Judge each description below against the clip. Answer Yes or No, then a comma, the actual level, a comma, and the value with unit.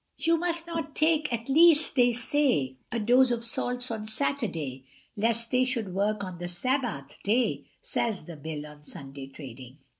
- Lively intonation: Yes, wide, 8.2 semitones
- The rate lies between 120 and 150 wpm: No, average, 170 wpm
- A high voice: Yes, high, 230 Hz